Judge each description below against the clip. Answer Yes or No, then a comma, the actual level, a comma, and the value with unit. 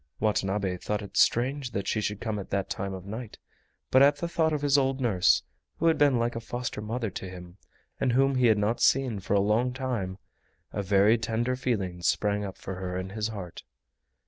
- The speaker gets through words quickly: Yes, fast, 215 wpm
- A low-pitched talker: Yes, low, 110 Hz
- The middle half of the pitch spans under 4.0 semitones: No, average, 4.6 semitones